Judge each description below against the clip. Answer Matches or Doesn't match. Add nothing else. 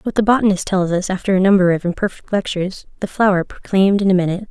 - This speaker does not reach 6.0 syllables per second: Doesn't match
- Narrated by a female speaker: Matches